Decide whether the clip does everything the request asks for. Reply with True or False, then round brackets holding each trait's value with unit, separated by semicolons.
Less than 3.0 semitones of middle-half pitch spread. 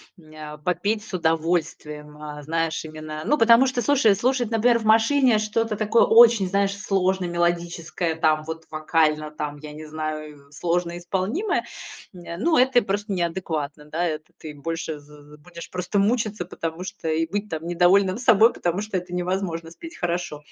False (5.1 semitones)